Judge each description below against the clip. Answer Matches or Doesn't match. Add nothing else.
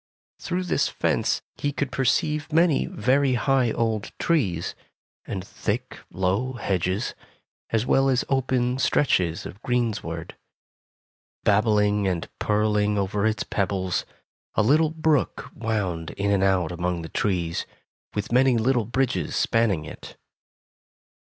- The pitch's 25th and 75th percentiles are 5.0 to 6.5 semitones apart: Matches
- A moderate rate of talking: Doesn't match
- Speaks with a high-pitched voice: Doesn't match